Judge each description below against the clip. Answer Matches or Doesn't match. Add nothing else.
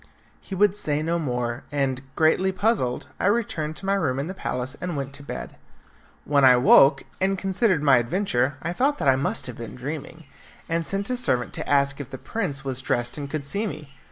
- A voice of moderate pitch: Matches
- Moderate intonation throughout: Doesn't match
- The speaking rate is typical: Doesn't match